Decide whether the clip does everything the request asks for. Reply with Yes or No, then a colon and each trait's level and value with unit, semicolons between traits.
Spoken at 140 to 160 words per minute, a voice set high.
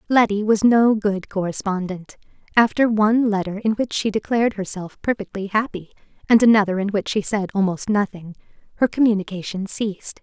Yes: average, 155 wpm; high, 205 Hz